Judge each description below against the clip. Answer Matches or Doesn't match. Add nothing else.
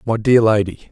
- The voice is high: Doesn't match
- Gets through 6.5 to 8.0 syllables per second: Doesn't match